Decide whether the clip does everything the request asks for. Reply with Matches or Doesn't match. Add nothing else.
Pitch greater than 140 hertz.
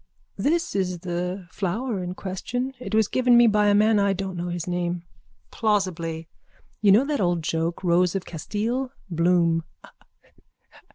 Matches